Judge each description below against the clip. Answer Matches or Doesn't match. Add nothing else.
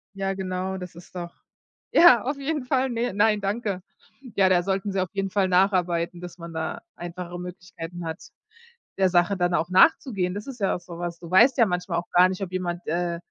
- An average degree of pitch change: Doesn't match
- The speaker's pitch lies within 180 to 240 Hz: Matches